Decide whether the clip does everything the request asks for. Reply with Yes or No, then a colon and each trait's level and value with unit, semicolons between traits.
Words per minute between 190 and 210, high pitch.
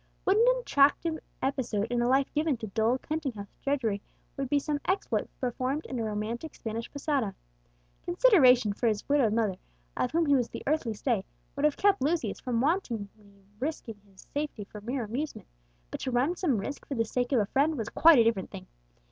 Yes: average, 200 wpm; very high, 255 Hz